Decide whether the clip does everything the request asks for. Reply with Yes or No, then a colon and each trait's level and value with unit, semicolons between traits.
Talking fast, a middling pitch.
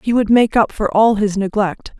No: fast, 240 wpm; high, 210 Hz